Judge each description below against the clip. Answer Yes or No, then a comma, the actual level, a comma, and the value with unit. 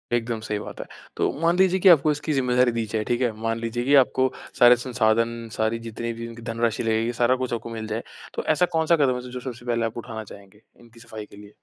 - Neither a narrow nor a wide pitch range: No, narrow, 2.1 semitones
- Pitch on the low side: Yes, low, 115 Hz